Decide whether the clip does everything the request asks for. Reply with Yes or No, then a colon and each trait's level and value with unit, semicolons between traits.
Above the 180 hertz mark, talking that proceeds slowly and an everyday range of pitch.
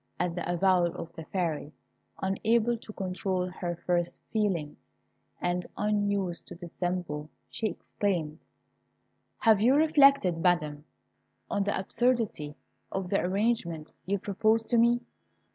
Yes: high, 190 Hz; slow, 125 wpm; average, 3.9 semitones